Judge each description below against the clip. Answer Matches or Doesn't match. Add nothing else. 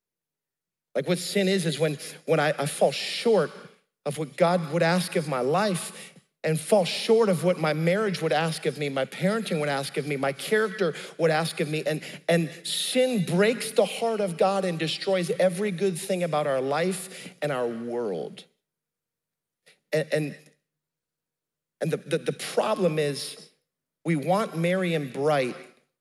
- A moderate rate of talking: Matches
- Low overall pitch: Doesn't match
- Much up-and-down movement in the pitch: Doesn't match